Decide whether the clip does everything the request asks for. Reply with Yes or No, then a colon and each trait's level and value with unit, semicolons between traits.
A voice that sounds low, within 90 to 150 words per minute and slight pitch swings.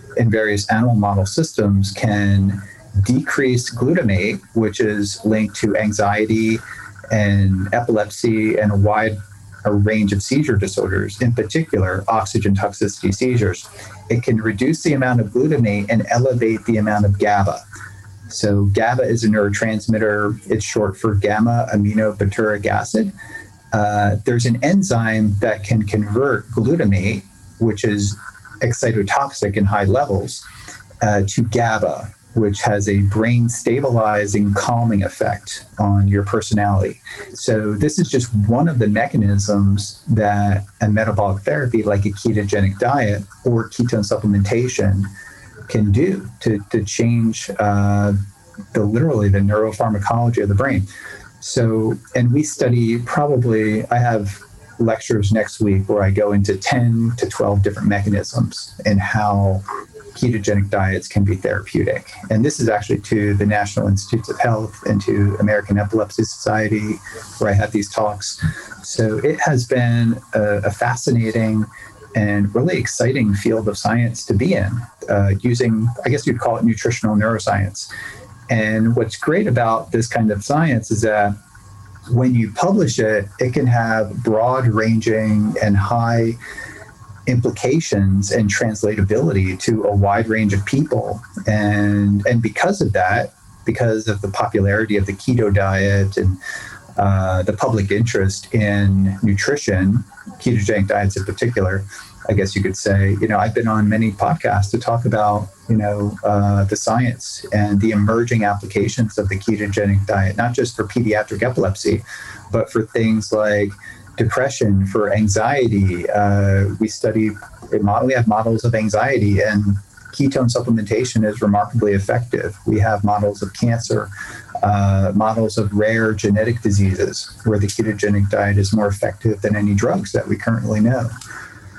Yes: low, 105 Hz; average, 145 wpm; narrow, 2.1 semitones